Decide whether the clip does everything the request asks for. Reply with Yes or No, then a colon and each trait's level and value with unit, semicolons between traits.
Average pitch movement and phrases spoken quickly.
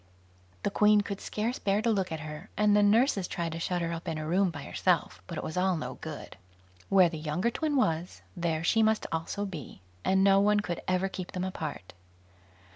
Yes: average, 4.0 semitones; fast, 215 wpm